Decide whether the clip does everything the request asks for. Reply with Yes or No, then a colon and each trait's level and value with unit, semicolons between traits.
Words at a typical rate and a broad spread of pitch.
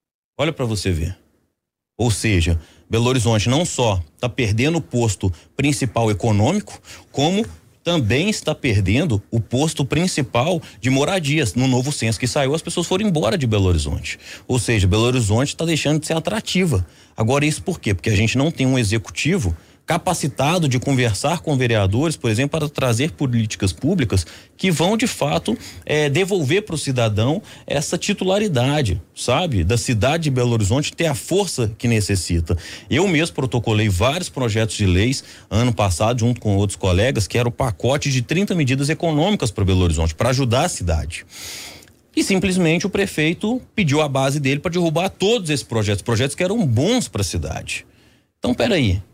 Yes: average, 170 wpm; wide, 6.6 semitones